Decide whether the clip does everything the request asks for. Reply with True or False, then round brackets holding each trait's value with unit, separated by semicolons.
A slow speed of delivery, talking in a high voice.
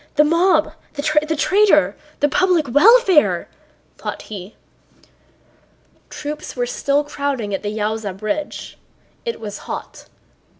True (115 wpm; 290 Hz)